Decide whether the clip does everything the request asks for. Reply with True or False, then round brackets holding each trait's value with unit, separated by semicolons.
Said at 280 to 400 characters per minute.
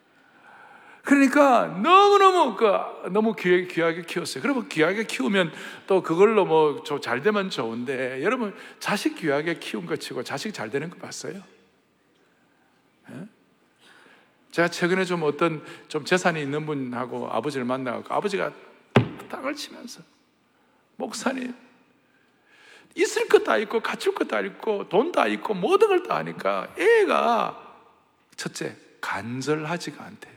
False (265 characters per minute)